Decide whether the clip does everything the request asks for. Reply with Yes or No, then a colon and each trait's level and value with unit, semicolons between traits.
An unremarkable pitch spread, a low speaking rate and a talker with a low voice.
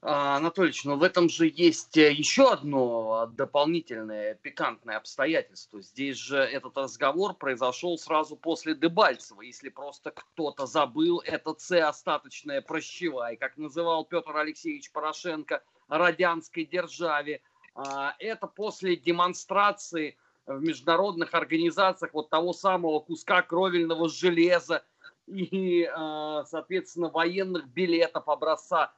No: average, 3.1 semitones; slow, 105 wpm; medium, 165 Hz